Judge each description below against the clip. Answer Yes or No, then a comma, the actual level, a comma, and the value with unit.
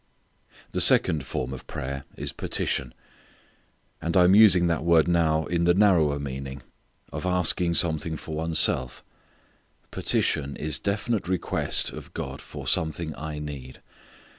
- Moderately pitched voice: No, very low, 80 Hz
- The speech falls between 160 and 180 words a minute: No, average, 145 wpm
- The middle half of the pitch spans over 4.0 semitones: No, average, 3.6 semitones